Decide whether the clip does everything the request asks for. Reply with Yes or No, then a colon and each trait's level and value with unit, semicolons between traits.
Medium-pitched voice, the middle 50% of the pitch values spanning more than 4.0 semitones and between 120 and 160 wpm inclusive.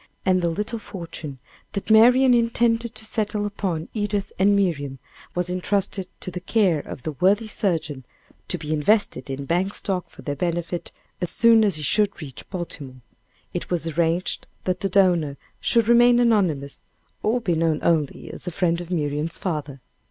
No: medium, 180 Hz; average, 4.7 semitones; average, 170 wpm